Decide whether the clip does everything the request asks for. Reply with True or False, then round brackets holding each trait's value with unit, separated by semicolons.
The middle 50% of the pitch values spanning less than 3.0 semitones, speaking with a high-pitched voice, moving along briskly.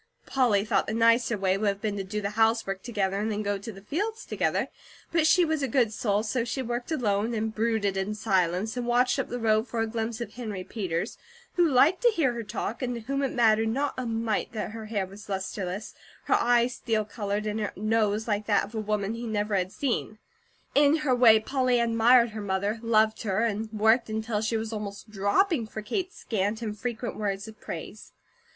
True (2.6 semitones; 220 Hz; 215 wpm)